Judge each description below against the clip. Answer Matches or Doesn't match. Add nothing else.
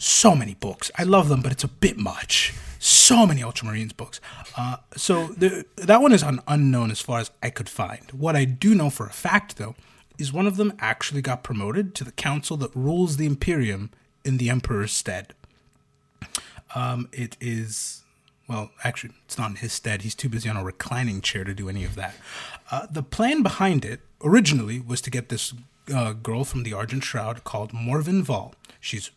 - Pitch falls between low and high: Doesn't match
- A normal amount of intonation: Matches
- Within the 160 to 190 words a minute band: Doesn't match